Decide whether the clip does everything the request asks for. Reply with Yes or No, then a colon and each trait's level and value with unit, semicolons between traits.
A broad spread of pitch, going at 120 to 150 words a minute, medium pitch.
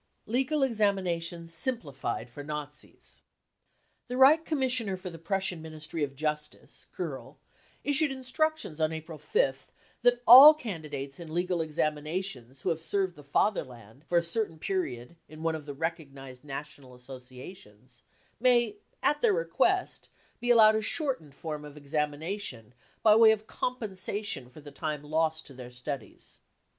Yes: wide, 7.0 semitones; average, 145 wpm; medium, 165 Hz